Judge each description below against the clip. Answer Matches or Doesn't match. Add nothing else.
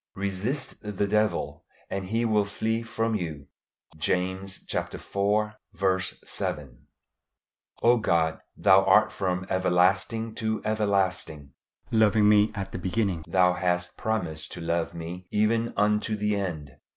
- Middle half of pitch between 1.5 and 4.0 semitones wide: Matches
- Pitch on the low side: Matches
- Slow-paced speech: Matches